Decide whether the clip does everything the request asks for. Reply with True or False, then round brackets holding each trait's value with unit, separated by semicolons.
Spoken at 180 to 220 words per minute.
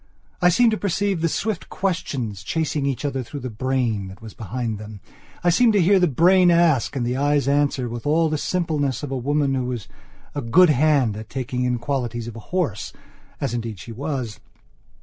True (200 wpm)